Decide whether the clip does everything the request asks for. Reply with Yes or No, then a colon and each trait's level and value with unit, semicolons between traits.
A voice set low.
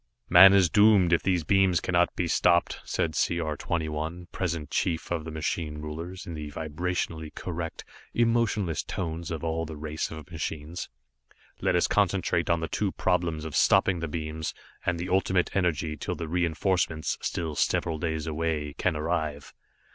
Yes: very low, 85 Hz